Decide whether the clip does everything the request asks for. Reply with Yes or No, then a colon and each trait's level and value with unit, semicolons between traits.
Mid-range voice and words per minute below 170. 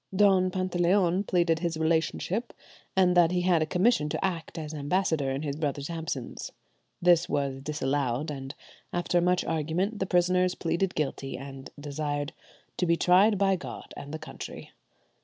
Yes: medium, 165 Hz; average, 160 wpm